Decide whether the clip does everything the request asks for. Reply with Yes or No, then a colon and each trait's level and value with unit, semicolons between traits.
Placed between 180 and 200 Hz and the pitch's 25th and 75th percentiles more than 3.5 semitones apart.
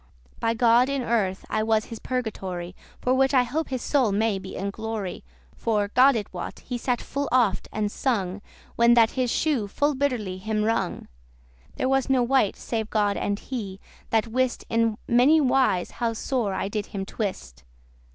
No: high, 225 Hz; average, 4.1 semitones